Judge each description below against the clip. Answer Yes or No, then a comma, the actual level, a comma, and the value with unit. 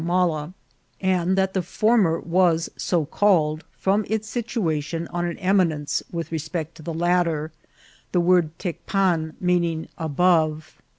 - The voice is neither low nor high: Yes, medium, 170 Hz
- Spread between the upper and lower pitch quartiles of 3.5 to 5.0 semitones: No, average, 2.7 semitones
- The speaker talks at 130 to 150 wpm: Yes, average, 140 wpm